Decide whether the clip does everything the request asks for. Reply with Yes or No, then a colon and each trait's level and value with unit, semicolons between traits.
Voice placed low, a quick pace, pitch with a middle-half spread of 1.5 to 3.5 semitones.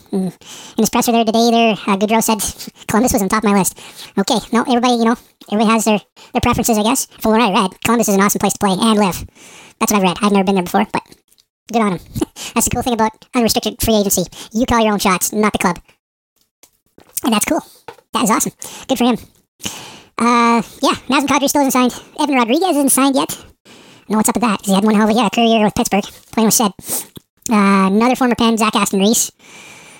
No: high, 225 Hz; fast, 230 wpm; average, 2.8 semitones